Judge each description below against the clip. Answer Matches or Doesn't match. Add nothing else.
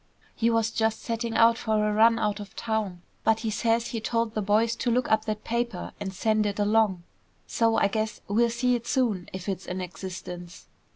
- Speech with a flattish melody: Matches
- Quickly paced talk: Matches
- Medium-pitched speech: Doesn't match